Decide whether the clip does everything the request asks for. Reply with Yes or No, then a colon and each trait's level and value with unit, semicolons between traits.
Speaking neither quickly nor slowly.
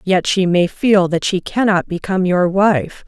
Yes: average, 195 wpm